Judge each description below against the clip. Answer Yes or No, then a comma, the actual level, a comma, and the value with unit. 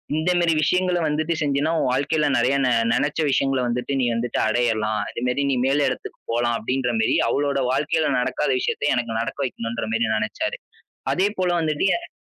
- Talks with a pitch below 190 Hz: Yes, low, 135 Hz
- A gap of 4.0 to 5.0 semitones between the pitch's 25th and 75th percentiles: Yes, average, 4.4 semitones